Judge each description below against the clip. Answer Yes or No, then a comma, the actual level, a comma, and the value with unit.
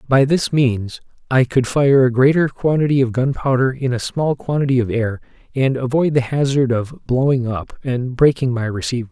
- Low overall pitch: Yes, low, 130 Hz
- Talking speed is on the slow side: No, average, 185 wpm